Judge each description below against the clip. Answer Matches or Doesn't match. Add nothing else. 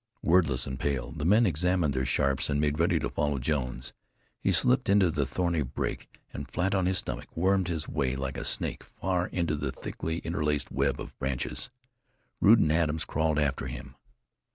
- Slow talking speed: Doesn't match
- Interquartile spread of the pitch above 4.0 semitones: Matches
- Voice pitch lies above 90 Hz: Doesn't match